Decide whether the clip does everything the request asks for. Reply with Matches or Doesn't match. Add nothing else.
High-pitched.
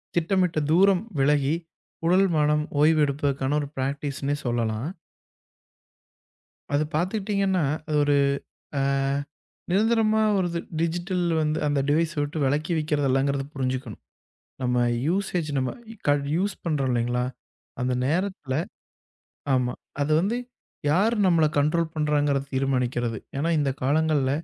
Doesn't match